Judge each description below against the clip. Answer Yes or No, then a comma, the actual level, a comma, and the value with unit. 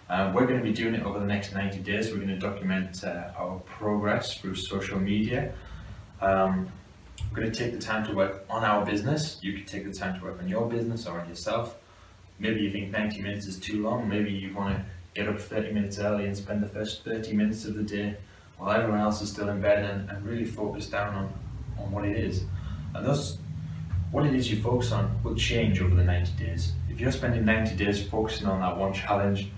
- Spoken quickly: Yes, fast, 230 wpm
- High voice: No, low, 100 Hz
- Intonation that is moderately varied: No, narrow, 1.9 semitones